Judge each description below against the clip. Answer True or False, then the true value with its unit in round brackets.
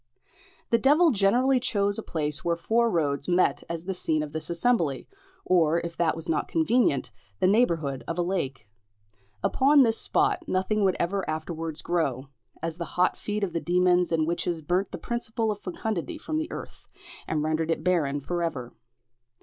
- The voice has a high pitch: False (175 Hz)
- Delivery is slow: False (180 wpm)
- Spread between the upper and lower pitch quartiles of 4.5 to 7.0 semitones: True (5.1 semitones)